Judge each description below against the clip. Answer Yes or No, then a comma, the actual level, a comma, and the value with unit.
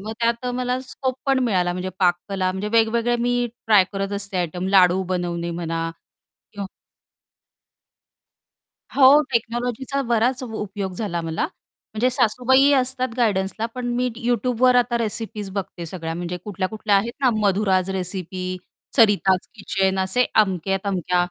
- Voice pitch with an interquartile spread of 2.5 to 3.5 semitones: No, average, 4.6 semitones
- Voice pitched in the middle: No, high, 205 Hz